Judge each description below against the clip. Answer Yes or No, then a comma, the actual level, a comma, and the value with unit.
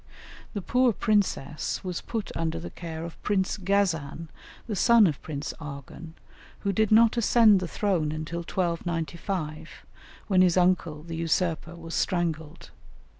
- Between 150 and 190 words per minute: No, average, 140 wpm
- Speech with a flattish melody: No, average, 3.6 semitones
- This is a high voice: No, medium, 170 Hz